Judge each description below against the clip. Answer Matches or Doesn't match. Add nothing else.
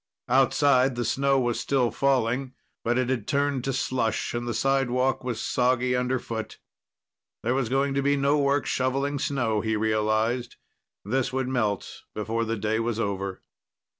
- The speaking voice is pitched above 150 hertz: Doesn't match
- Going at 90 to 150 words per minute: Doesn't match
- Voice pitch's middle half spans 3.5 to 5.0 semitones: Doesn't match